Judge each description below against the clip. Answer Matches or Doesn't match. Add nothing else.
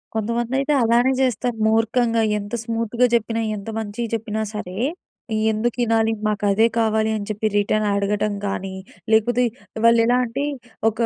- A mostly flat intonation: Matches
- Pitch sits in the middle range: Doesn't match